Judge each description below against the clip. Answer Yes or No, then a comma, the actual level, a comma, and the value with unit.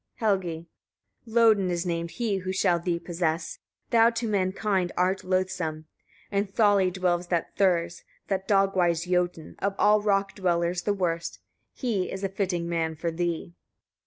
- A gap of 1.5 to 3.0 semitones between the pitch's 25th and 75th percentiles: Yes, narrow, 2.5 semitones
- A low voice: No, medium, 185 Hz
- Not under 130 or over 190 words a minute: Yes, average, 160 wpm